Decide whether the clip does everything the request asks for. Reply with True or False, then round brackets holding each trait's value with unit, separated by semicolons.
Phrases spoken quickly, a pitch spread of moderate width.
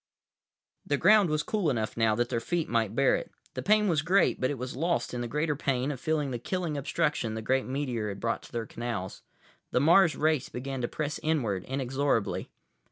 True (215 wpm; 4.6 semitones)